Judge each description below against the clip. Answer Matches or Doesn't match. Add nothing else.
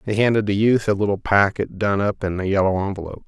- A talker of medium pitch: Doesn't match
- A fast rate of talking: Matches